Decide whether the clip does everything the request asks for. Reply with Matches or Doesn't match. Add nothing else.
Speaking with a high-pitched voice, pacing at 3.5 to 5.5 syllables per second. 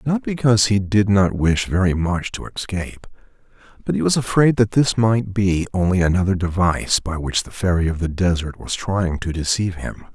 Doesn't match